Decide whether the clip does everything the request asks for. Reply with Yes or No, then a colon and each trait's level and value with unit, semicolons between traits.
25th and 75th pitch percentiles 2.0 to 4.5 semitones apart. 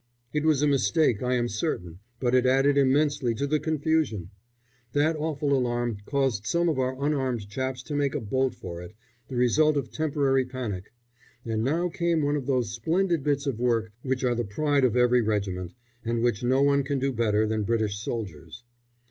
Yes: average, 4.1 semitones